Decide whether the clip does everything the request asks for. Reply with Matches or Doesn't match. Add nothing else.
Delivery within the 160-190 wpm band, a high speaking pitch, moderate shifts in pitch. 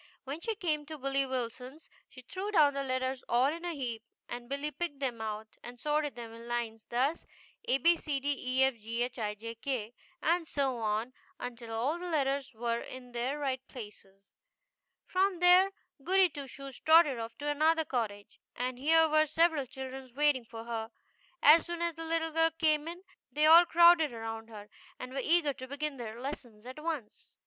Matches